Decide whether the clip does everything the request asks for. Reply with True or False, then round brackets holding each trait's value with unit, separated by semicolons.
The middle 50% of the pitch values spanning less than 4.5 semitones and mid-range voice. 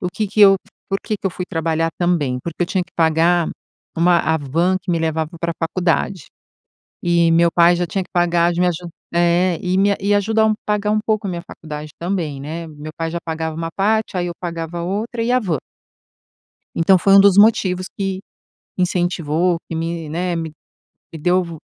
True (2.6 semitones; 175 Hz)